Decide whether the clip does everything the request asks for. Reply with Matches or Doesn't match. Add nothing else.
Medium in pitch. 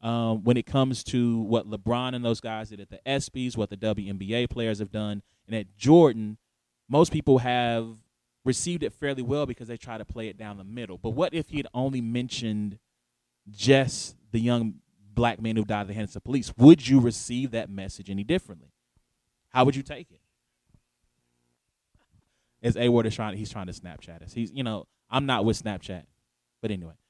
Doesn't match